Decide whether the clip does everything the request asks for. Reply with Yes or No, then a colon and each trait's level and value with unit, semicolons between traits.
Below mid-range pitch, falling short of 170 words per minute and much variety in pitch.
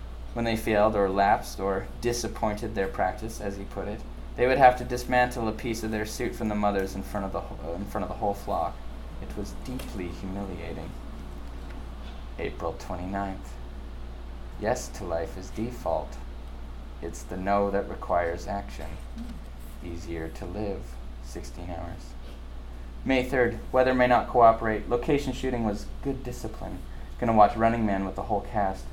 Yes: very low, 90 Hz; average, 160 wpm; wide, 8.0 semitones